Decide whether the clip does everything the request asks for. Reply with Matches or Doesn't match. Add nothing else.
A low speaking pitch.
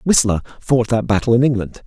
Matches